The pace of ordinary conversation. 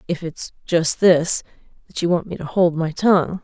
Yes: average, 190 wpm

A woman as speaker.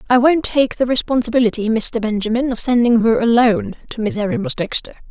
Yes: female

